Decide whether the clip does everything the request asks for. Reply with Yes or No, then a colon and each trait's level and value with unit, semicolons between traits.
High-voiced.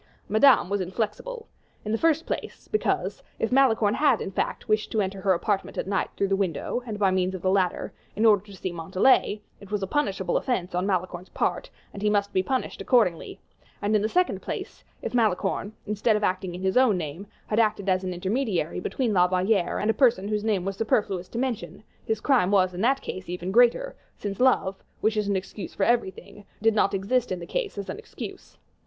Yes: high, 205 Hz